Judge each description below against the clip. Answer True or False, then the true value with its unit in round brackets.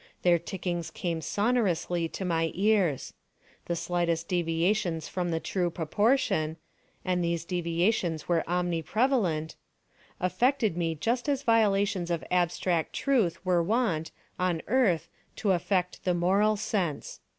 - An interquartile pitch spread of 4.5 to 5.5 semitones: False (3.5 semitones)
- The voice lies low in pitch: False (180 Hz)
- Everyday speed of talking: False (120 wpm)